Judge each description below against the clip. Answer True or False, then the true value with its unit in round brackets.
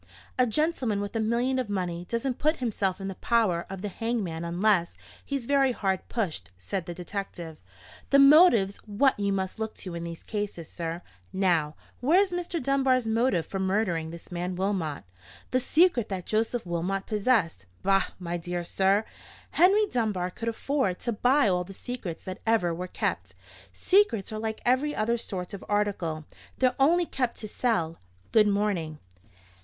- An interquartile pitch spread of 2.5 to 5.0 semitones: False (5.5 semitones)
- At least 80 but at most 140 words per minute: False (170 wpm)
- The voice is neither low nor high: False (205 Hz)